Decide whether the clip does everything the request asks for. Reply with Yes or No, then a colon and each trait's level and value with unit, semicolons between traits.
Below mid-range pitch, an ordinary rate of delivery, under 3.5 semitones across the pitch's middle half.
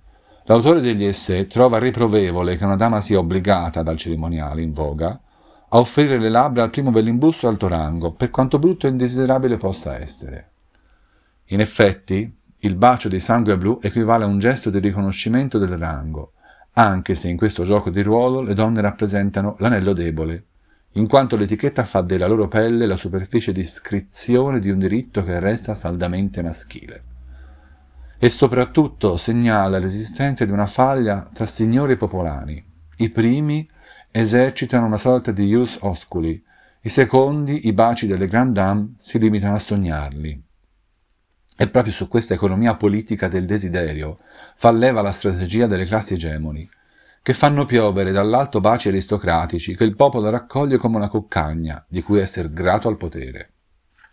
No: low, 105 Hz; average, 155 wpm; average, 4.7 semitones